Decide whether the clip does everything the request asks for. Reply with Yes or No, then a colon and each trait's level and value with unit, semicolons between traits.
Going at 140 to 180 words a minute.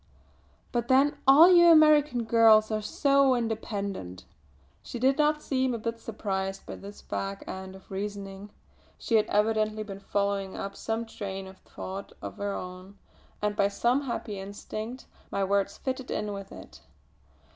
Yes: average, 155 wpm